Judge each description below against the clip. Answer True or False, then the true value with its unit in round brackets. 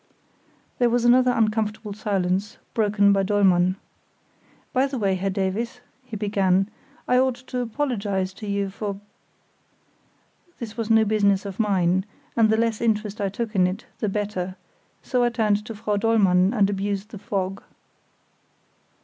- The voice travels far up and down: False (2.6 semitones)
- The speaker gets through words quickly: False (150 wpm)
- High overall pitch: True (210 Hz)